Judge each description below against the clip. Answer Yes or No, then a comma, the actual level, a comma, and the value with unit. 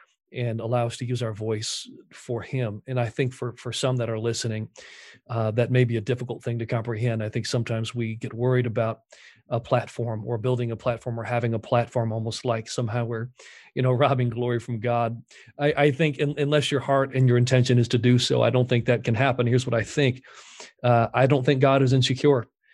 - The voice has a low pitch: Yes, low, 120 Hz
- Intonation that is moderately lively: No, narrow, 1.7 semitones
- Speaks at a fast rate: Yes, fast, 225 wpm